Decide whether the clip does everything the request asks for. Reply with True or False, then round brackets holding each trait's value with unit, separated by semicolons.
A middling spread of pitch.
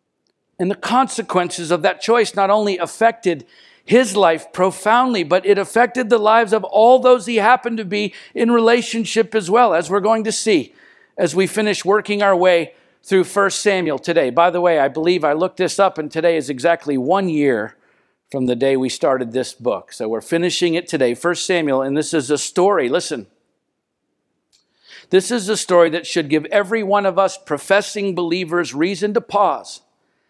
True (4.4 semitones)